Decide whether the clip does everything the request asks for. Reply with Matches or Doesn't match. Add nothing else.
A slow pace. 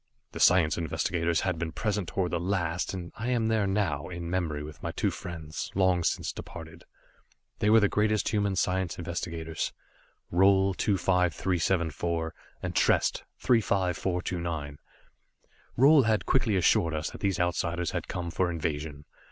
Doesn't match